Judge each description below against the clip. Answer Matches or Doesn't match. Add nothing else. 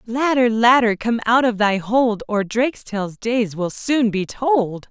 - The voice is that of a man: Doesn't match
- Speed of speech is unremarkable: Matches